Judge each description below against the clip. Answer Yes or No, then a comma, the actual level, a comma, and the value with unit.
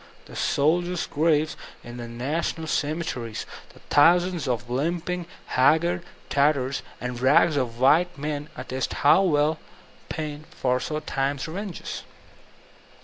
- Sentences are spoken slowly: Yes, slow, 115 wpm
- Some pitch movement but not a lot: Yes, average, 4.2 semitones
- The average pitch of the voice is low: No, medium, 150 Hz